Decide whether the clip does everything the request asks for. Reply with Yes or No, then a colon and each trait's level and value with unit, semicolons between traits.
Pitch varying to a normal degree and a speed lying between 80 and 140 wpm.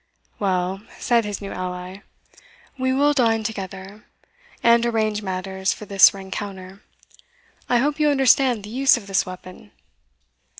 Yes: average, 3.9 semitones; slow, 135 wpm